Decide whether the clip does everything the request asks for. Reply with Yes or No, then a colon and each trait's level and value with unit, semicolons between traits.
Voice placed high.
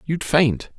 No: medium, 145 Hz